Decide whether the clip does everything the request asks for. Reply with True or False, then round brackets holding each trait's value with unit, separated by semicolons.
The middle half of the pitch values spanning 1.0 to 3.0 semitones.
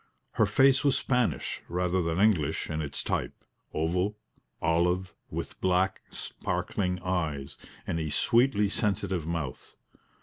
False (3.9 semitones)